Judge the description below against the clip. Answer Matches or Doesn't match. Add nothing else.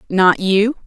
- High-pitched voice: Matches